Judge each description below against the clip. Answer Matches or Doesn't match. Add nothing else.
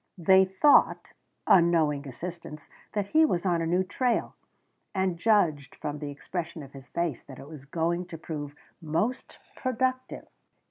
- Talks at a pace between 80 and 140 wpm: Doesn't match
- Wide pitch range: Doesn't match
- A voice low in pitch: Doesn't match